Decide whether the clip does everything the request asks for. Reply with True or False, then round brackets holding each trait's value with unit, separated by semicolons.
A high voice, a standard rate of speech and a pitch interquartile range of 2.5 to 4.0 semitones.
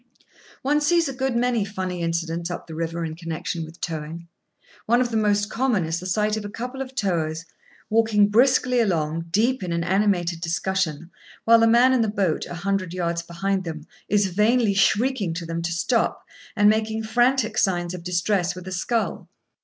False (195 Hz; 190 wpm; 5.0 semitones)